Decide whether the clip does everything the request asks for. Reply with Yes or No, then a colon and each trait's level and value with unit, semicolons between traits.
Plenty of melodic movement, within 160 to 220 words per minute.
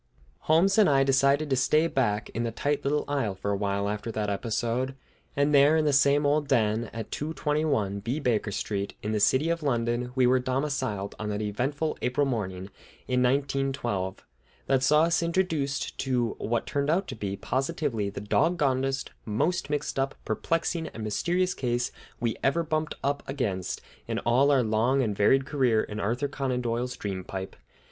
No: average, 4.9 semitones; average, 180 wpm